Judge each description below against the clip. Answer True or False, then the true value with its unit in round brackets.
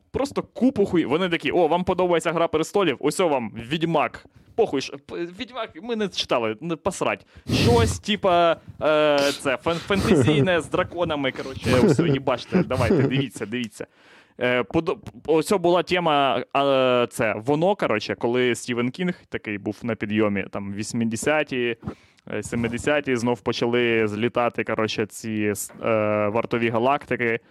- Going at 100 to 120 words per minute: False (135 wpm)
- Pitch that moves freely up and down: True (6.3 semitones)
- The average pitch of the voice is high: False (135 Hz)